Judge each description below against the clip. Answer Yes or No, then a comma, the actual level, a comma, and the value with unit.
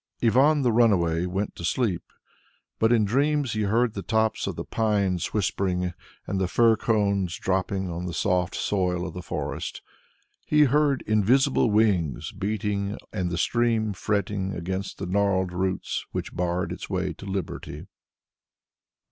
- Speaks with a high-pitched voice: No, low, 100 Hz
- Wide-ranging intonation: No, average, 3.5 semitones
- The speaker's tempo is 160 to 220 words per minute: No, average, 150 wpm